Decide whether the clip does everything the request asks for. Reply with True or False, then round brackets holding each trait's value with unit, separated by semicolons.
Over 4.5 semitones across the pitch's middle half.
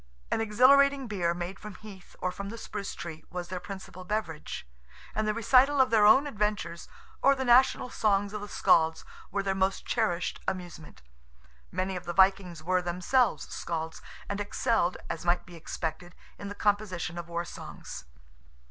False (3.6 semitones)